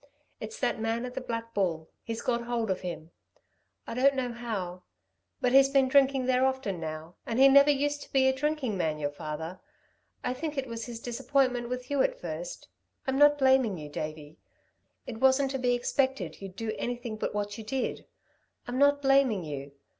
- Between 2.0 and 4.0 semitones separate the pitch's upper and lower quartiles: No, average, 5.3 semitones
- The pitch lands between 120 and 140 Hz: No, high, 245 Hz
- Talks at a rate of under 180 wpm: No, average, 195 wpm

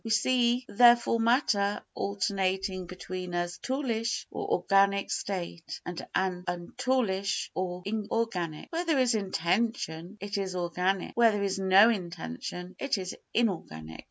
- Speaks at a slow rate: Yes, slow, 130 wpm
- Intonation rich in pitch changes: No, average, 4.2 semitones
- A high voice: Yes, high, 195 Hz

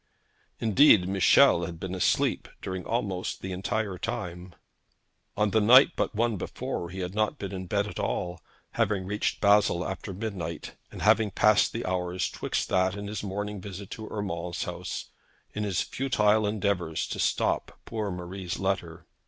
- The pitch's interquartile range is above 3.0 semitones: No, average, 2.7 semitones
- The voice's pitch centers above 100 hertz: No, very low, 95 Hz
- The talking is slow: No, average, 160 wpm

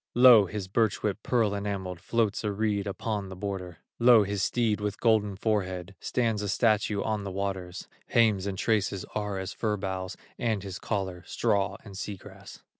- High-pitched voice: No, low, 100 Hz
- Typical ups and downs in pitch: No, narrow, 2.1 semitones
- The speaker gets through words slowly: No, average, 180 wpm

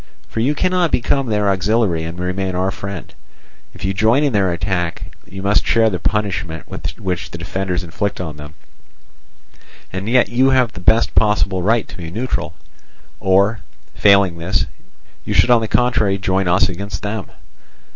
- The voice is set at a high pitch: No, very low, 95 Hz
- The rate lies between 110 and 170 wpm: Yes, average, 165 wpm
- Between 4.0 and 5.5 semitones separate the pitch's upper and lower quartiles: No, average, 3.6 semitones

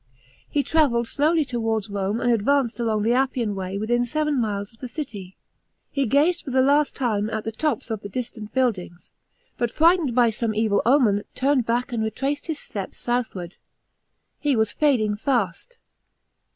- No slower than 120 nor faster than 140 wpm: No, average, 170 wpm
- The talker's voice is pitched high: Yes, high, 235 Hz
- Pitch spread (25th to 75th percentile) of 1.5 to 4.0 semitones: No, average, 4.5 semitones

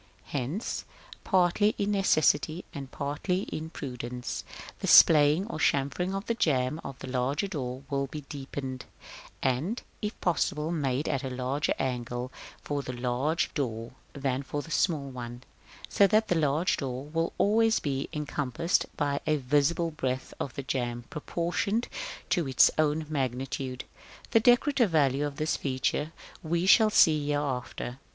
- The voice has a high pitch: No, medium, 145 Hz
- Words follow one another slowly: No, average, 145 wpm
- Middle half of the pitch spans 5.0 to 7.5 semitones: No, average, 4.3 semitones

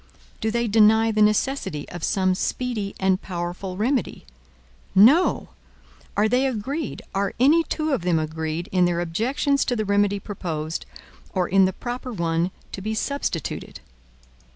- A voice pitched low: No, high, 205 Hz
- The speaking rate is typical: Yes, average, 150 wpm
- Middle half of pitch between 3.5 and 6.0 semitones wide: Yes, wide, 5.4 semitones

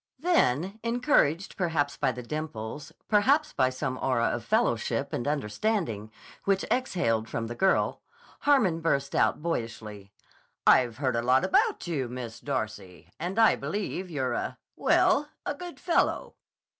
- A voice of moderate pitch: Yes, medium, 145 Hz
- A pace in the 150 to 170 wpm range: No, average, 140 wpm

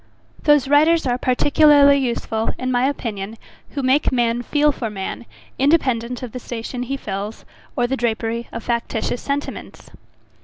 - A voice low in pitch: No, very high, 250 Hz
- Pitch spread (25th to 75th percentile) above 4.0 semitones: No, average, 3.4 semitones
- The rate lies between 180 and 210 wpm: No, average, 150 wpm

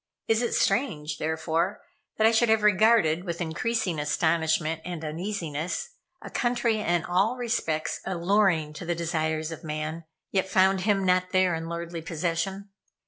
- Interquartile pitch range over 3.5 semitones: Yes, average, 4.0 semitones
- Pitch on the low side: No, medium, 175 Hz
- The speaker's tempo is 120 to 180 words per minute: Yes, average, 150 wpm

